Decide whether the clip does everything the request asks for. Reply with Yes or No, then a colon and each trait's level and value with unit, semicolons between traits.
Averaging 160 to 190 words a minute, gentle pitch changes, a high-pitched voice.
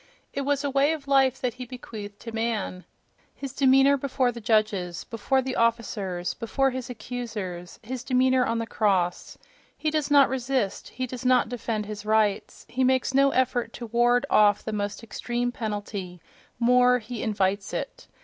No: average, 165 wpm; average, 3.5 semitones; high, 240 Hz